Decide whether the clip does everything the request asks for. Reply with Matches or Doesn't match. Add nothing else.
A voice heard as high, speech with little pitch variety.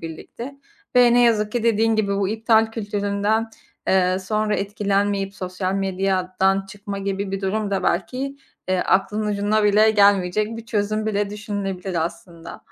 Matches